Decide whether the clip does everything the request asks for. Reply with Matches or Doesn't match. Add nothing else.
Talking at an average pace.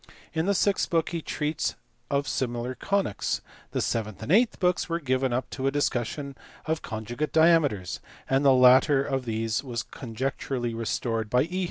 Matches